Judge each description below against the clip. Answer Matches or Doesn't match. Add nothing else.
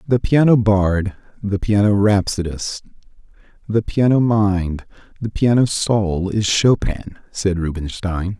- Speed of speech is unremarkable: Doesn't match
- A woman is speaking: Doesn't match